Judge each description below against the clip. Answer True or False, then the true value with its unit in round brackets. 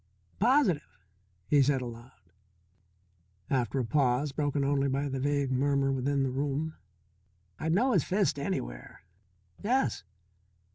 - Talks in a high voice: False (140 Hz)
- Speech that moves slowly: True (125 wpm)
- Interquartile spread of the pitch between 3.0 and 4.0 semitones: False (2.4 semitones)